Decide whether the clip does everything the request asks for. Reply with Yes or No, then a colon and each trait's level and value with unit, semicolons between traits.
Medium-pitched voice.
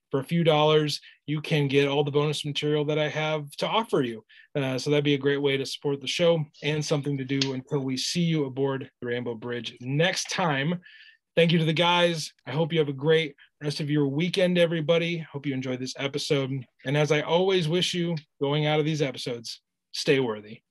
Yes: medium, 150 Hz